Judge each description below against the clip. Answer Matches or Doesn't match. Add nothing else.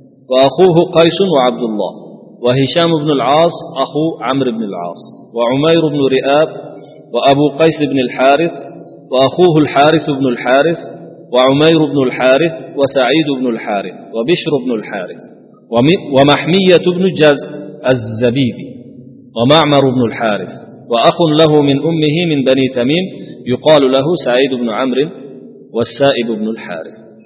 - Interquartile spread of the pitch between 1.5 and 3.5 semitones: Doesn't match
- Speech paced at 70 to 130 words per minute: Matches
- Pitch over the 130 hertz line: Matches